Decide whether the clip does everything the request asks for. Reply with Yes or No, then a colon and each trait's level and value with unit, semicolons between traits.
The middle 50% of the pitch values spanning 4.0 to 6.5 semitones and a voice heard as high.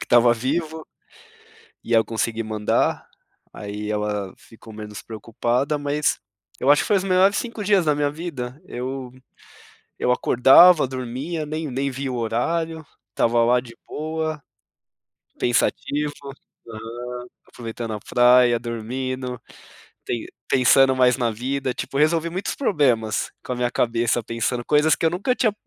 No: average, 4.6 semitones; low, 130 Hz